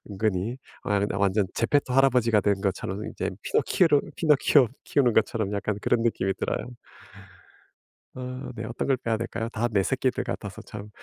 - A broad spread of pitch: No, average, 3.8 semitones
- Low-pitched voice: Yes, low, 115 Hz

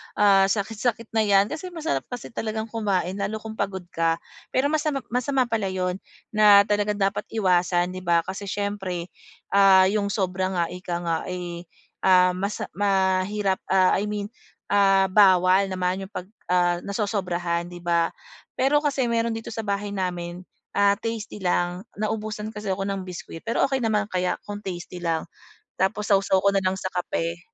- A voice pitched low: No, high, 195 Hz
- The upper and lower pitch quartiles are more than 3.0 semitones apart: No, average, 2.7 semitones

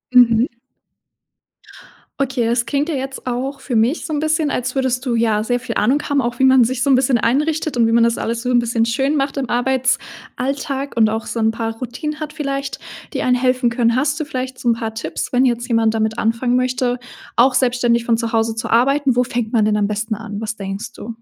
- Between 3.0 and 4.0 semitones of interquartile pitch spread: No, narrow, 2.6 semitones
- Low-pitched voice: No, high, 245 Hz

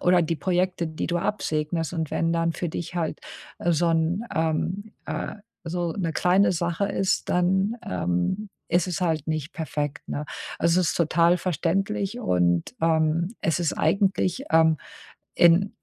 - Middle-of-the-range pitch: Yes, medium, 170 Hz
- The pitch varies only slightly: Yes, narrow, 2.3 semitones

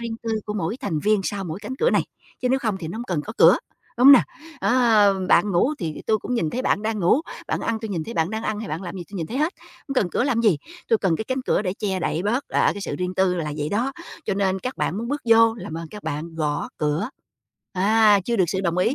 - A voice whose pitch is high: Yes, high, 205 Hz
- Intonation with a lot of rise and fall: No, average, 4.8 semitones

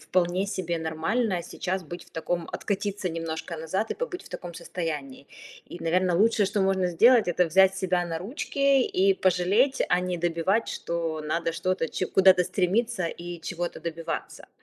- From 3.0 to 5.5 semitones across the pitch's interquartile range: No, narrow, 2.5 semitones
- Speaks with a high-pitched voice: No, medium, 180 Hz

